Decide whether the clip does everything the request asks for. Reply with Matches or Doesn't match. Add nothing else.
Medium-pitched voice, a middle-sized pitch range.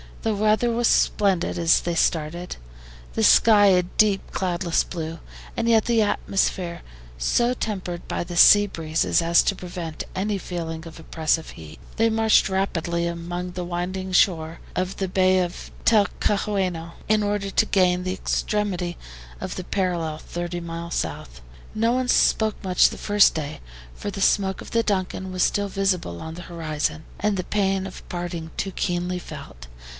Matches